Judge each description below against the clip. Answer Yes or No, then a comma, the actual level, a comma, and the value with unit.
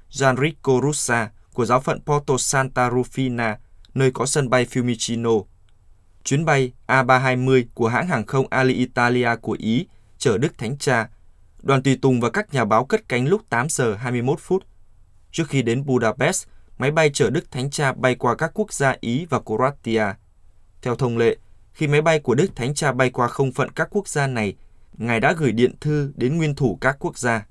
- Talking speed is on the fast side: No, average, 190 wpm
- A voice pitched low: Yes, low, 125 Hz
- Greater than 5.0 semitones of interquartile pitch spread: No, average, 3.4 semitones